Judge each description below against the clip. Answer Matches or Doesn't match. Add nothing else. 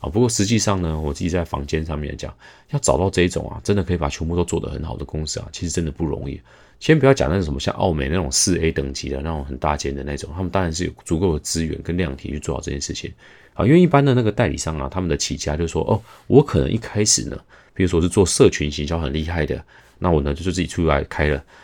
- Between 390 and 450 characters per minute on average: Matches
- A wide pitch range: Doesn't match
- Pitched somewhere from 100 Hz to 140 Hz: Doesn't match